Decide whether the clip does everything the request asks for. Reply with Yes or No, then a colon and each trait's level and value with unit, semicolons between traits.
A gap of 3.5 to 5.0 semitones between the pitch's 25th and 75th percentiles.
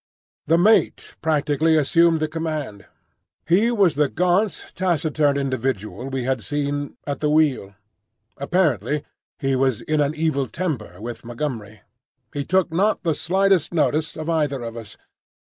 Yes: average, 3.8 semitones